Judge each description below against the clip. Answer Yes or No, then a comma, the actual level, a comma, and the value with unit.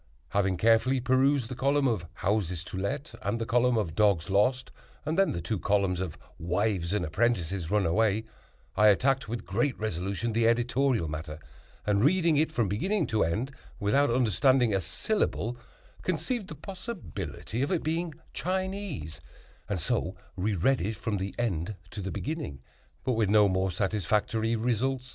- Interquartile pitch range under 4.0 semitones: No, wide, 5.5 semitones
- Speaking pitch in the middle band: No, low, 110 Hz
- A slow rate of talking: No, average, 160 wpm